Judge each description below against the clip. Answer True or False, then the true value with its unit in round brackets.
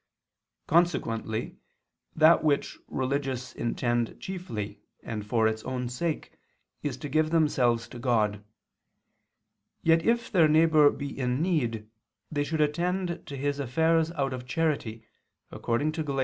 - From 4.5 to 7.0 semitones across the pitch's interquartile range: True (5.1 semitones)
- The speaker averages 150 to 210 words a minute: False (135 wpm)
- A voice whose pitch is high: False (140 Hz)